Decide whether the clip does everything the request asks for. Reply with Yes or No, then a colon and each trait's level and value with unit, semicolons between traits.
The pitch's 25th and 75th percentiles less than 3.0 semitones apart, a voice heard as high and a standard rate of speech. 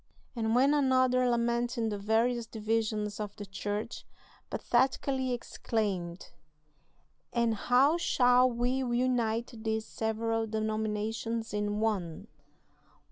No: narrow, 2.4 semitones; high, 225 Hz; slow, 100 wpm